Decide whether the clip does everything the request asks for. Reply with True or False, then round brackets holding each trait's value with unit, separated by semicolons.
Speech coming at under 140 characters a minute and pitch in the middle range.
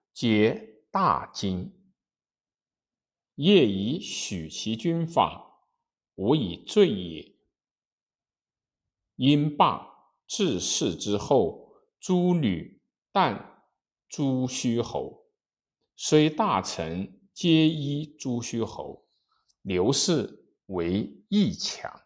True (105 characters per minute; 150 Hz)